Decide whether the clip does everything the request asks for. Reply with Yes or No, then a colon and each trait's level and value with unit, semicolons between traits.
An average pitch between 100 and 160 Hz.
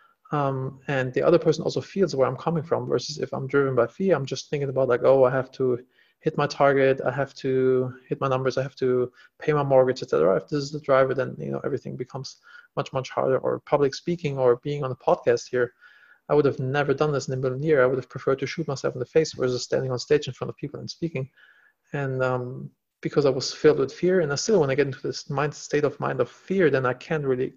Yes: low, 135 Hz